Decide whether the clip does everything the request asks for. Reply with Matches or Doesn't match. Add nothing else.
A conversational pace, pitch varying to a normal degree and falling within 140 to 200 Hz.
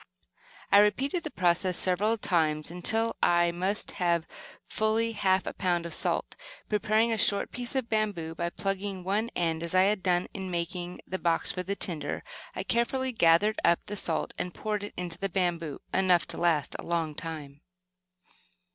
Matches